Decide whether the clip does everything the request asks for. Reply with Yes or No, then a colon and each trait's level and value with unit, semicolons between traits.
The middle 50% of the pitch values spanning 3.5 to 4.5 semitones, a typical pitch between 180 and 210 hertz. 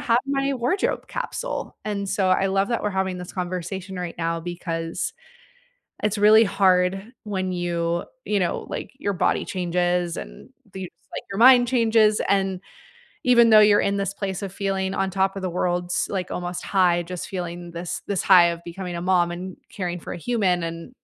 No: narrow, 2.5 semitones; high, 190 Hz